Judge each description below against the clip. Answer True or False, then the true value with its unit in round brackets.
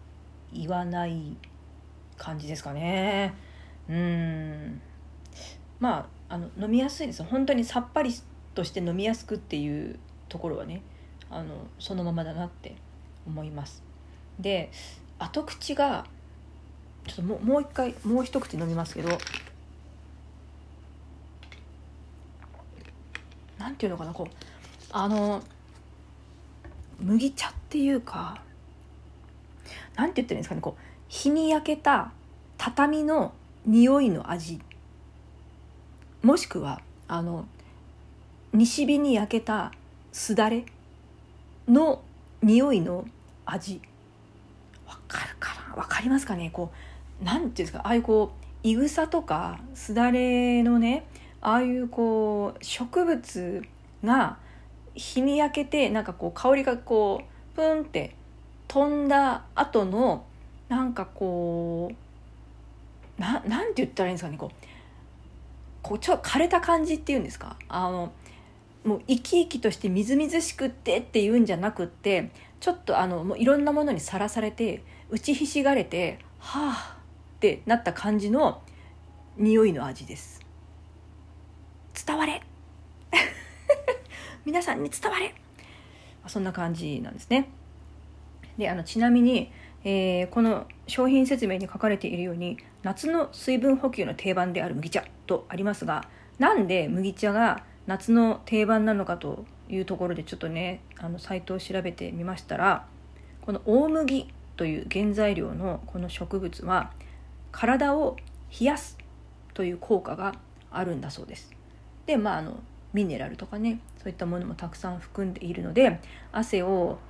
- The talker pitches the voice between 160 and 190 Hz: True (185 Hz)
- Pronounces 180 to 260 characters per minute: True (255 characters per minute)